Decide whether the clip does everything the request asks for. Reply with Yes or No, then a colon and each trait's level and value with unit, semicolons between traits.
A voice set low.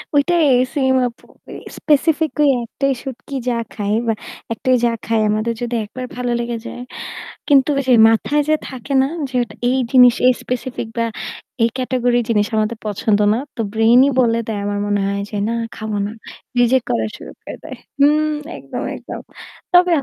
No: high, 240 Hz